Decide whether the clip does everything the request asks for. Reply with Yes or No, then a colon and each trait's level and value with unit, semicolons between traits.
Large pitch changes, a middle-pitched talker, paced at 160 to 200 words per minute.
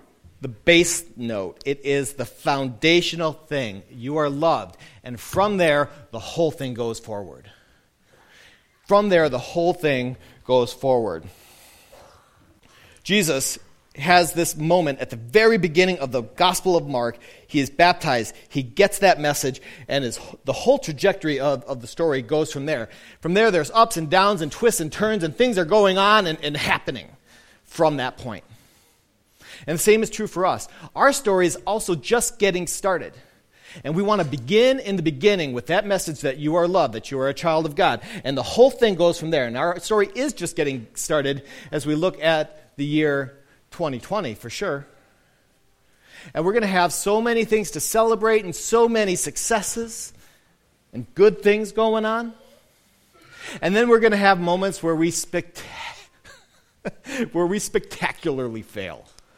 Yes: wide, 6.4 semitones; medium, 165 Hz; average, 175 wpm